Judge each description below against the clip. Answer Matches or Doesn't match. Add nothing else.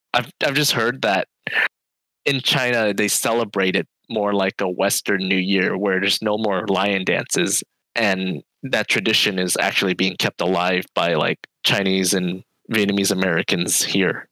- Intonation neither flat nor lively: Doesn't match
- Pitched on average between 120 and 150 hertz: Doesn't match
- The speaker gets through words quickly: Doesn't match